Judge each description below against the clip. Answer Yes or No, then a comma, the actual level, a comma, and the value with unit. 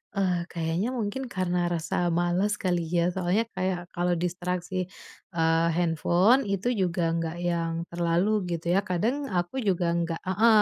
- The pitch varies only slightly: Yes, narrow, 1.9 semitones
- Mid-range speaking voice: Yes, medium, 175 Hz